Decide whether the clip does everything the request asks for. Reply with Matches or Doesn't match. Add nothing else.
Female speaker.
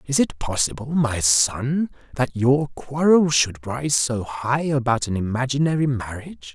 Doesn't match